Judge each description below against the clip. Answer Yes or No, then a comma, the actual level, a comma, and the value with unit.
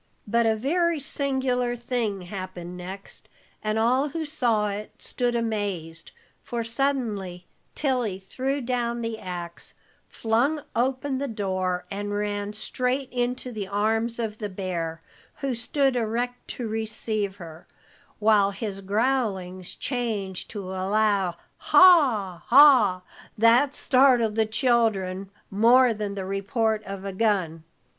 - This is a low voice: No, high, 220 Hz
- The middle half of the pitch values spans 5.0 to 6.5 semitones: No, average, 4.1 semitones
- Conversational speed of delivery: No, slow, 130 wpm